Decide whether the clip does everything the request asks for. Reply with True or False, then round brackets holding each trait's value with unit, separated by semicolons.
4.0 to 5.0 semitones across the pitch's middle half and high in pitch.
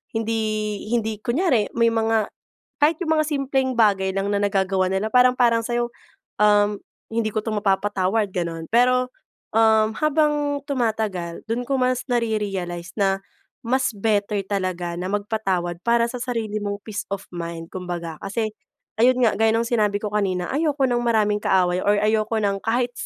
False (3.4 semitones; 215 Hz)